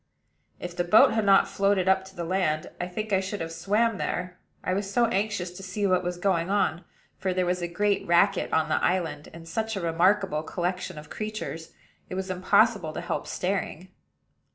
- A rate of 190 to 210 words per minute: Yes, average, 200 wpm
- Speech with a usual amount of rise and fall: No, narrow, 2.3 semitones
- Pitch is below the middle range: No, medium, 185 Hz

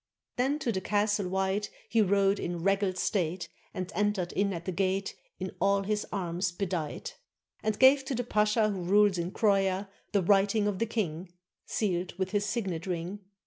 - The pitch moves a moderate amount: No, narrow, 2.2 semitones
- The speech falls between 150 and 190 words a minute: Yes, average, 180 wpm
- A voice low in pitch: No, high, 195 Hz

